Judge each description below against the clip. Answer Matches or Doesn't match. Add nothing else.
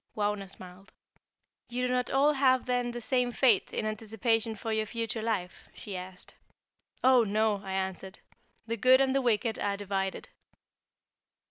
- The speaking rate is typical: Matches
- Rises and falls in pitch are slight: Doesn't match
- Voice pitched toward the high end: Matches